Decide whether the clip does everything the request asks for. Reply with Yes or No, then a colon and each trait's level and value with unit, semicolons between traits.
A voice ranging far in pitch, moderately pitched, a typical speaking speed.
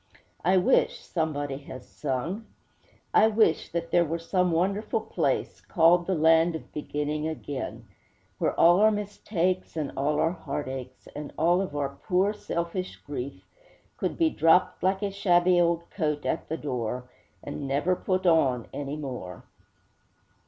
No: average, 4.0 semitones; medium, 165 Hz; average, 150 wpm